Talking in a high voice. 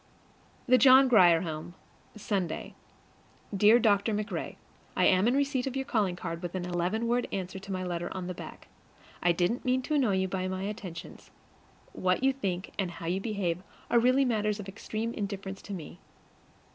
Yes: high, 195 Hz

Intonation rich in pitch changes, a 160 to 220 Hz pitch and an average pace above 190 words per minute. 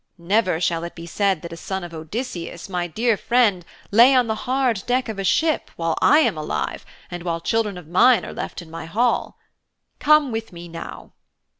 Yes: wide, 5.7 semitones; high, 190 Hz; average, 200 wpm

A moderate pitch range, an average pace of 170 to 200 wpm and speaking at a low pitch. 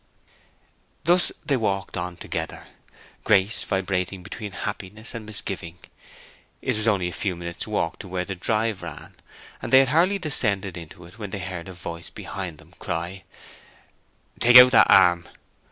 No: average, 3.7 semitones; average, 160 wpm; very low, 95 Hz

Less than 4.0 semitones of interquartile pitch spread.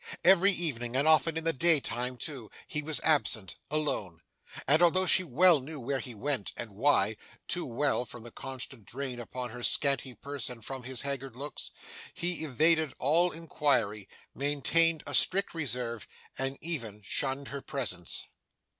No: average, 4.5 semitones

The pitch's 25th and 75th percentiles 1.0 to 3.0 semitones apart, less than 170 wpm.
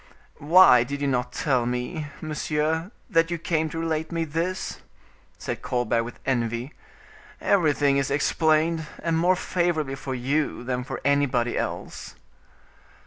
No: average, 4.3 semitones; average, 140 wpm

